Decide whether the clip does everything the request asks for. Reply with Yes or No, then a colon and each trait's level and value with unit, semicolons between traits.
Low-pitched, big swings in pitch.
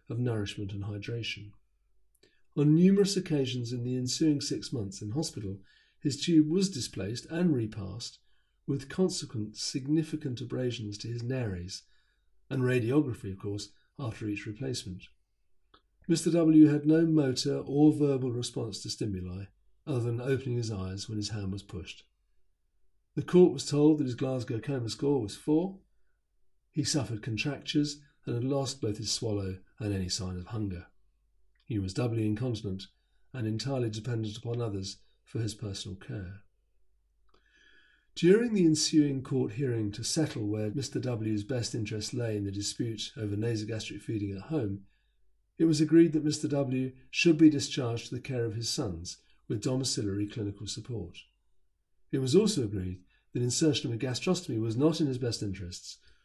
Yes: low, 120 Hz; wide, 6.1 semitones